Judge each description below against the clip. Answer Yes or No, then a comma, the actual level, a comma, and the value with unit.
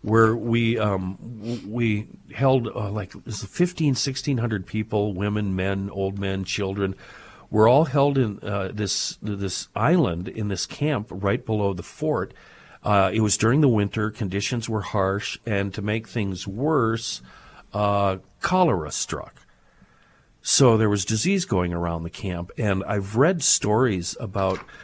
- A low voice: Yes, low, 105 Hz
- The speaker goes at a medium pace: Yes, average, 150 wpm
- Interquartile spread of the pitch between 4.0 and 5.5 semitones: No, average, 3.0 semitones